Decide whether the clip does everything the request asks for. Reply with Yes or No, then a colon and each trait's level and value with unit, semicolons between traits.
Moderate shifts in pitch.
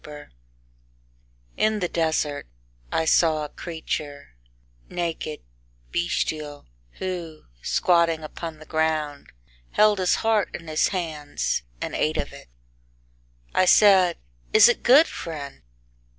Yes: average, 3.0 semitones